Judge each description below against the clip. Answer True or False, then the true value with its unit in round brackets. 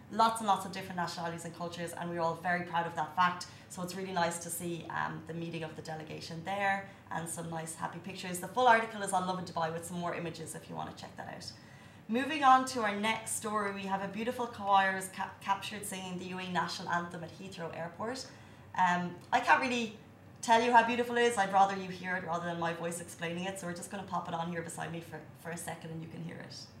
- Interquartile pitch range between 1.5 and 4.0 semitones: True (2.8 semitones)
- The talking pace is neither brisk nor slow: False (255 wpm)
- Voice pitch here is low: False (175 Hz)